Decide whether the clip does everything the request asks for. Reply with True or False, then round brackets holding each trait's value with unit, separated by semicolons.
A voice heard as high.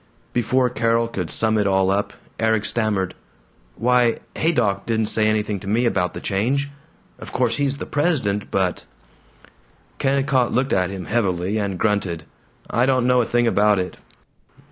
False (110 Hz)